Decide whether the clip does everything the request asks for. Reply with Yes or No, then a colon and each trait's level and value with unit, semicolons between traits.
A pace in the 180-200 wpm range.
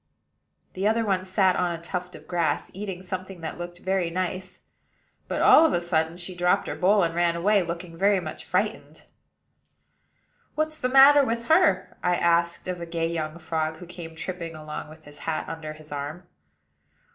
Yes: average, 185 wpm